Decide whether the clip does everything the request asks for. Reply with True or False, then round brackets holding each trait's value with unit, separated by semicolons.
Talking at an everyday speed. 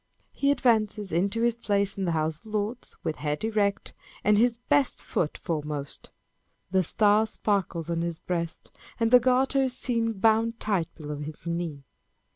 True (165 wpm)